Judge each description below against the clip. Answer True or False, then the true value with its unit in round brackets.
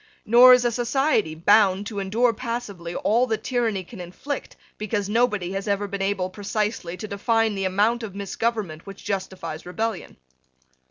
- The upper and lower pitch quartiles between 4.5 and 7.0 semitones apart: False (3.2 semitones)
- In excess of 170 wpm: False (160 wpm)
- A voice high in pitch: True (205 Hz)